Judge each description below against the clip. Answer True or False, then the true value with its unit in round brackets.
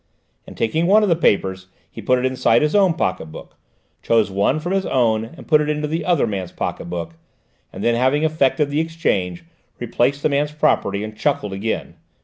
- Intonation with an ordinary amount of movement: False (7.1 semitones)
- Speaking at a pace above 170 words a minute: True (200 wpm)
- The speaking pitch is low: True (130 Hz)